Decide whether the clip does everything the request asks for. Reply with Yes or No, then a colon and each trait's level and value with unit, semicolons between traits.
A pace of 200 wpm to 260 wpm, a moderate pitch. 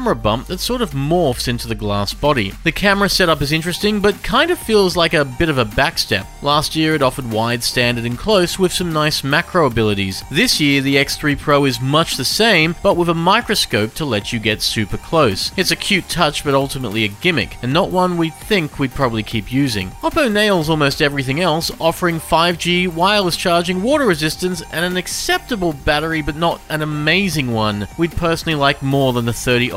Yes: fast, 205 wpm; medium, 155 Hz